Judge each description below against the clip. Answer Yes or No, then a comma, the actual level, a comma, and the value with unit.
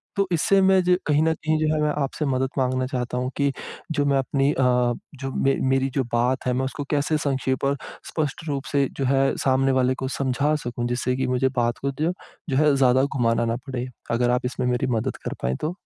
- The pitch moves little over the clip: Yes, narrow, 2.3 semitones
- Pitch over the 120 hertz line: Yes, low, 135 Hz